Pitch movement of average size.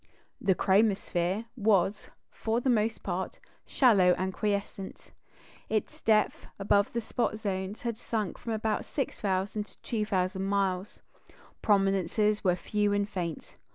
No: narrow, 2.3 semitones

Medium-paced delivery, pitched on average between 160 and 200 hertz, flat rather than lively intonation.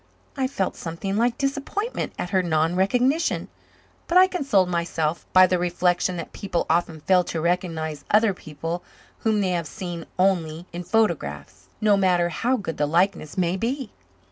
No: average, 165 wpm; medium, 185 Hz; average, 4.3 semitones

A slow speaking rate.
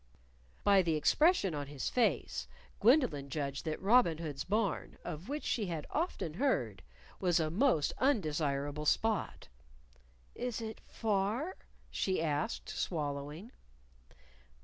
Yes: slow, 120 wpm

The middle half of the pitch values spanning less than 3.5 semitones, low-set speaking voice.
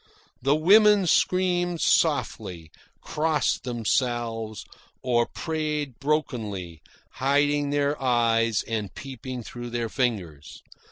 No: average, 4.9 semitones; low, 125 Hz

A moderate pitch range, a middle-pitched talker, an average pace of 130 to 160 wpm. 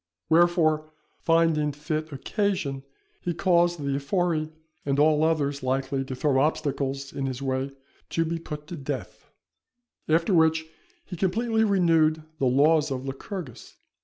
Yes: average, 3.3 semitones; medium, 155 Hz; slow, 135 wpm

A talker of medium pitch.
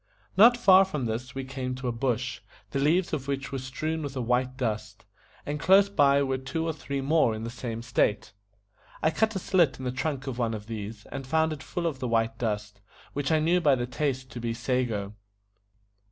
No: low, 130 Hz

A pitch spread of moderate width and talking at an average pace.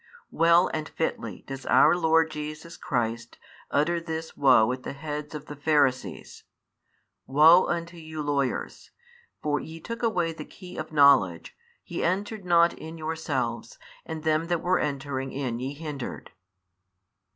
Yes: average, 3.0 semitones; average, 150 wpm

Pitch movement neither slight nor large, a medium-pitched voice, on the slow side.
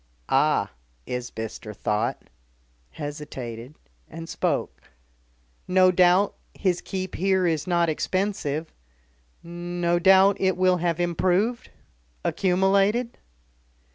Yes: average, 3.3 semitones; medium, 175 Hz; slow, 90 wpm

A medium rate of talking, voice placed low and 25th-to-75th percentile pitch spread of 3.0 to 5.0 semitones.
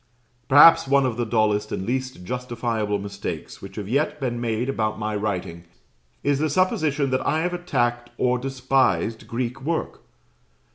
Yes: average, 155 wpm; low, 120 Hz; average, 4.1 semitones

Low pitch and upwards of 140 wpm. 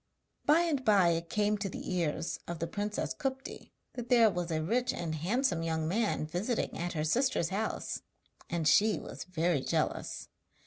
No: medium, 185 Hz; average, 175 wpm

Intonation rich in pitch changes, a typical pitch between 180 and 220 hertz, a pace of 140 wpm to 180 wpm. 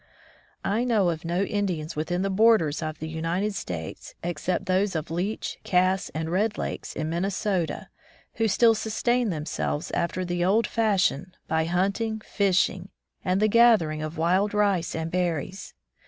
No: average, 4.1 semitones; medium, 185 Hz; average, 155 wpm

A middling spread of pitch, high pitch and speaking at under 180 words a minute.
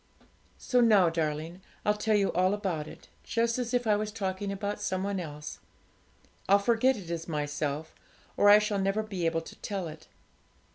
No: average, 4.3 semitones; high, 195 Hz; average, 185 wpm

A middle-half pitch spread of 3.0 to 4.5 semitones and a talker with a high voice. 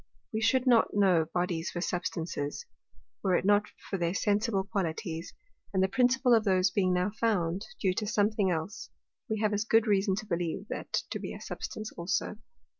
Yes: average, 3.3 semitones; high, 195 Hz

